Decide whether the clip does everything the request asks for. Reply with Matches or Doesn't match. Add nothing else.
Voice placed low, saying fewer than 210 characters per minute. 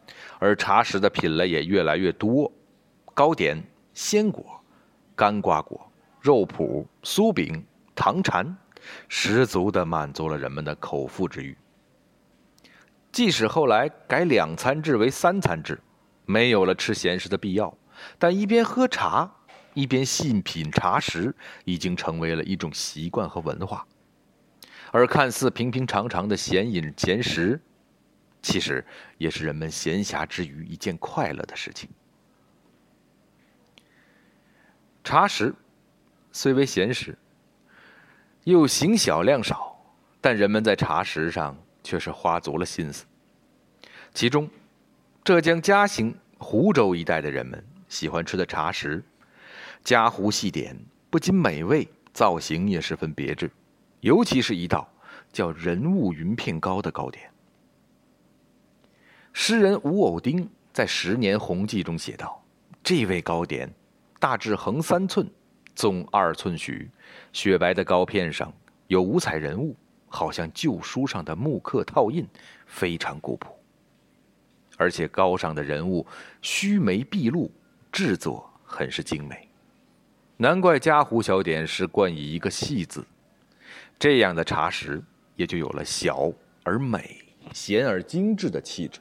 Matches